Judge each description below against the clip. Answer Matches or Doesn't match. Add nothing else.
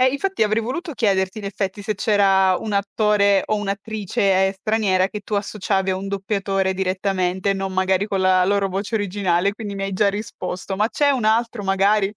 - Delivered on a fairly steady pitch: Matches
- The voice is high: Matches